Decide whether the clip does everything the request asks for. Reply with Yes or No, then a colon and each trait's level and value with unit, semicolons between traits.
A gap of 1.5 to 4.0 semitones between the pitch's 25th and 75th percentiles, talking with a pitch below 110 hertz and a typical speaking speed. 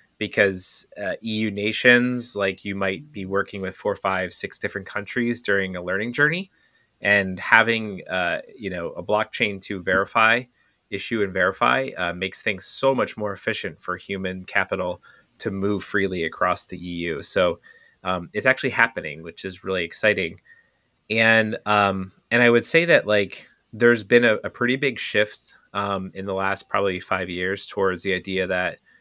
Yes: average, 3.2 semitones; low, 100 Hz; average, 170 wpm